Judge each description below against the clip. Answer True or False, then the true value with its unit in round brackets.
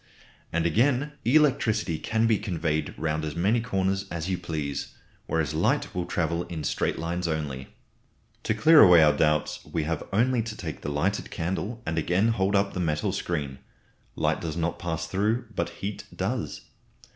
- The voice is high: False (85 Hz)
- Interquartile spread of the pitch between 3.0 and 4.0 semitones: False (4.9 semitones)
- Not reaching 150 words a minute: False (170 wpm)